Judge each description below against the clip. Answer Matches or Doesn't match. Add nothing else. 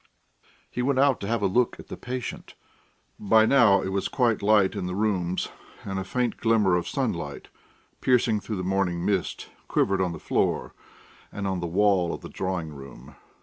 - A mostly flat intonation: Doesn't match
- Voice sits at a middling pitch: Doesn't match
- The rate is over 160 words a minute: Matches